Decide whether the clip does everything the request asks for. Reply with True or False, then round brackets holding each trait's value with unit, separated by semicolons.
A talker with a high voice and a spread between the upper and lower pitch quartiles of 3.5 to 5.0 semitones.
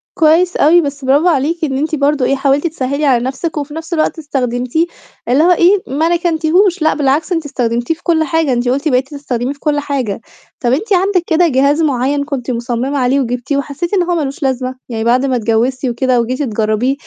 True (280 Hz; 4.0 semitones)